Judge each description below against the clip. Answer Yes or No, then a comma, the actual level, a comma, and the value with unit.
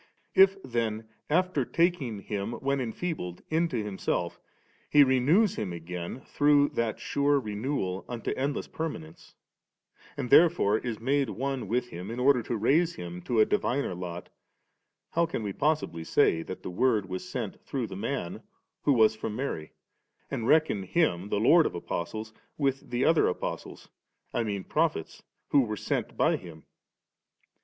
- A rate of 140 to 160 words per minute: Yes, average, 155 wpm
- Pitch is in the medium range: No, low, 120 Hz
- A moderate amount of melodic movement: No, wide, 6.4 semitones